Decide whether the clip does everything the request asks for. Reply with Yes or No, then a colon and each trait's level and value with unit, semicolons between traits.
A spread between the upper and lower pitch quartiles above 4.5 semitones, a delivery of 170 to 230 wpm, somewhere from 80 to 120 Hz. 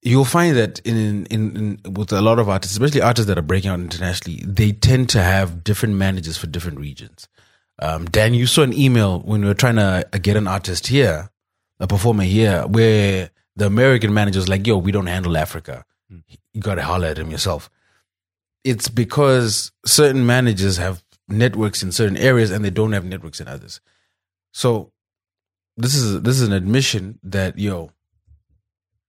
No: average, 3.6 semitones; average, 185 wpm; low, 100 Hz